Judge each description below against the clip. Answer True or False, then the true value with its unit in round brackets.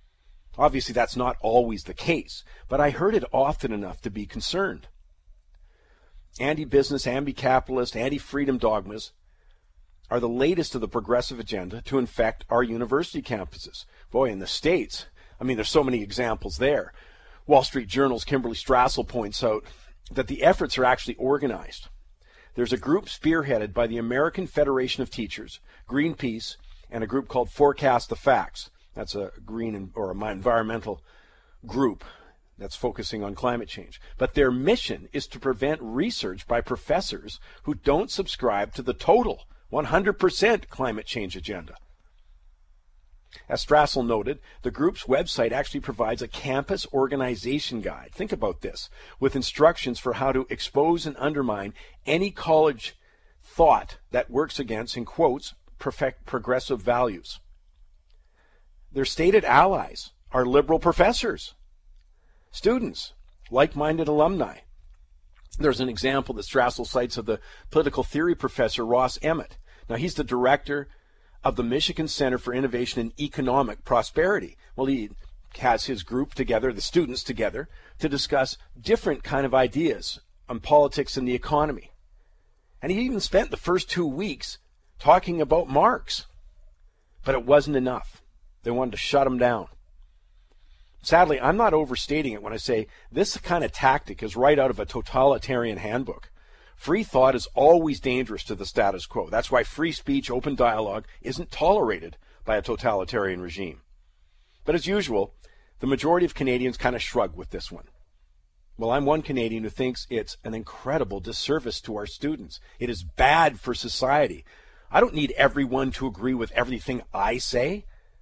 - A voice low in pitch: True (125 Hz)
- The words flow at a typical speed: True (150 wpm)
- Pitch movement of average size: True (5.0 semitones)